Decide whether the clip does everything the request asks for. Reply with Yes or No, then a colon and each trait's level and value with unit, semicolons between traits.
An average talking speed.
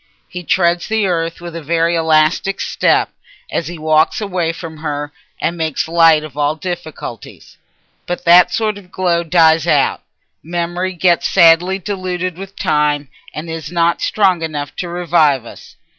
Yes: average, 160 wpm